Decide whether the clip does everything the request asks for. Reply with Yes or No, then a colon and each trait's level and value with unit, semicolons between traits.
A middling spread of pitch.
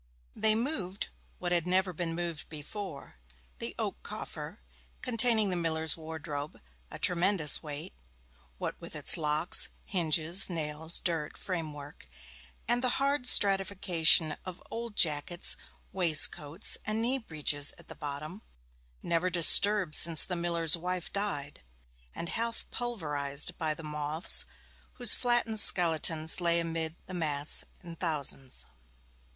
Yes: average, 4.0 semitones